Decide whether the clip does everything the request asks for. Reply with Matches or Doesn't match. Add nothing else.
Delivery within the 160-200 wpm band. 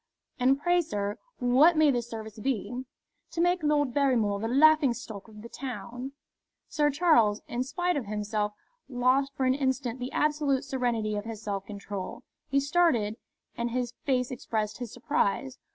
Matches